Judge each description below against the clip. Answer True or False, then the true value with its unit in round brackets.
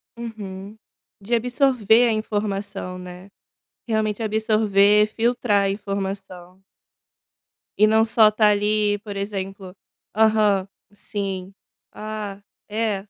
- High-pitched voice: True (210 Hz)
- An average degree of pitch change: False (1.8 semitones)